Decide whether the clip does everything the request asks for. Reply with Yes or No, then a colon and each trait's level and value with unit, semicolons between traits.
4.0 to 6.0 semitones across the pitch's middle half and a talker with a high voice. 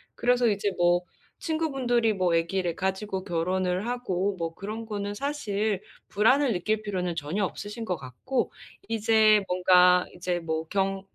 No: average, 3.6 semitones; high, 195 Hz